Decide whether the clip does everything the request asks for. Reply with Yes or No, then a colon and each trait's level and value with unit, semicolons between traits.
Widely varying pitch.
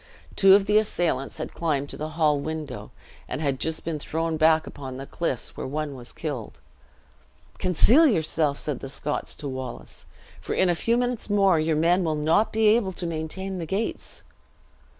No: average, 4.5 semitones